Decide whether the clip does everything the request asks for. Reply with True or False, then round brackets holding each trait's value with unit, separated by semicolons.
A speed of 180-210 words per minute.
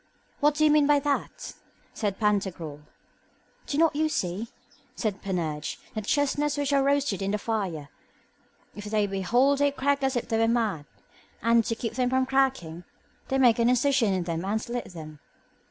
True (185 wpm)